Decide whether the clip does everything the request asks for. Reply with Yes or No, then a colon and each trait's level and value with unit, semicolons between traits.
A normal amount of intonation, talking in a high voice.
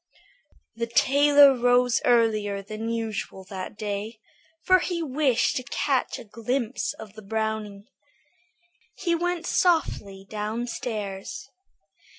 Yes: average, 4.4 semitones; high, 230 Hz